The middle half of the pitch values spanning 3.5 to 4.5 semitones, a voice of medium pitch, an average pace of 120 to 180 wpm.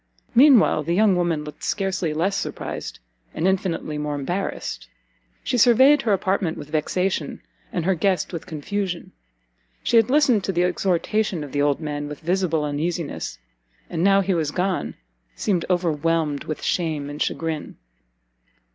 Yes: average, 4.2 semitones; medium, 175 Hz; average, 155 wpm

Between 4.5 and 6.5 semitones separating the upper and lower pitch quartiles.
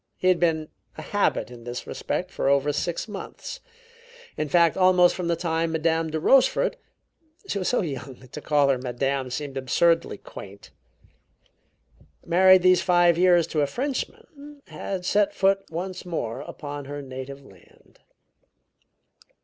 Yes: average, 4.8 semitones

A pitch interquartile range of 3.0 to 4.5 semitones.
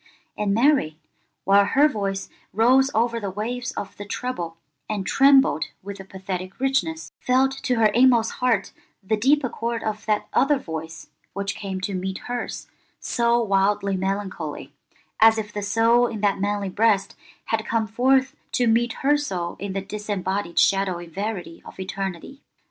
Yes: average, 3.9 semitones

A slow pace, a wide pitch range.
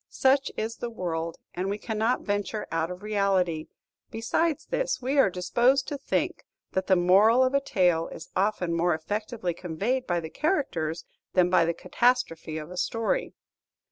No: average, 170 wpm; wide, 5.9 semitones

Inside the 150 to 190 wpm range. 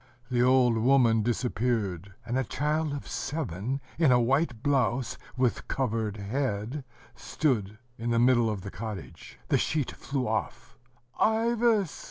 No: average, 140 wpm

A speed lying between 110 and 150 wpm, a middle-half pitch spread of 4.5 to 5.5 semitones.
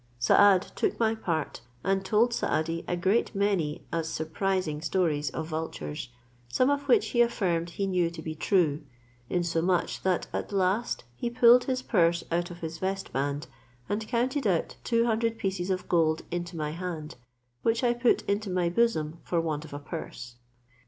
No: average, 170 wpm; average, 4.9 semitones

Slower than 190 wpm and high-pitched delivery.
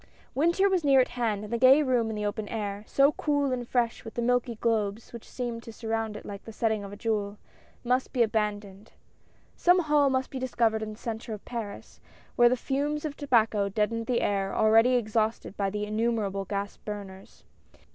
No: fast, 205 wpm; high, 225 Hz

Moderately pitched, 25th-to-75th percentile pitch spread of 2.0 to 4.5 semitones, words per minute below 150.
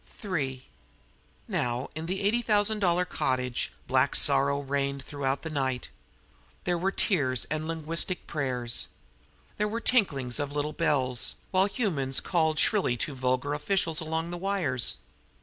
No: medium, 150 Hz; wide, 5.5 semitones; average, 140 wpm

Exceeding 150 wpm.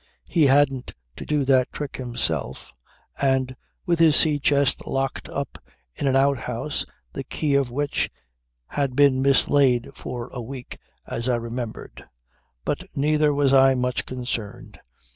No: average, 145 wpm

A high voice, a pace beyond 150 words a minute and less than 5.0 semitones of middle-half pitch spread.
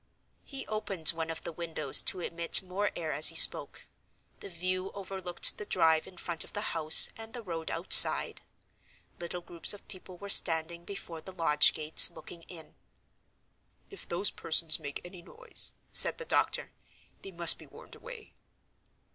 No: medium, 175 Hz; average, 165 wpm; average, 3.0 semitones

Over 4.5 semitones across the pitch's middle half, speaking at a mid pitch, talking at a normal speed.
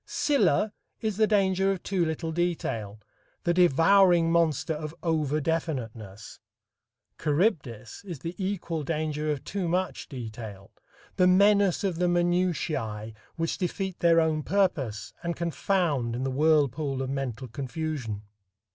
No: average, 5.1 semitones; medium, 160 Hz; slow, 130 wpm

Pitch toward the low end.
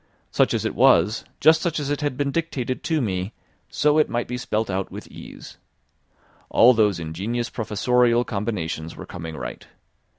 Yes: low, 120 Hz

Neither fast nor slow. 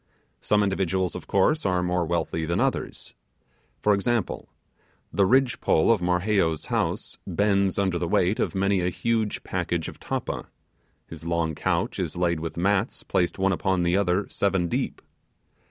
Yes: average, 160 wpm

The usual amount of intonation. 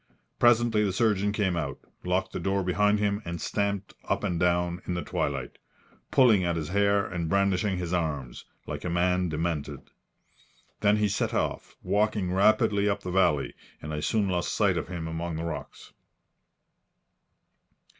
Yes: average, 3.0 semitones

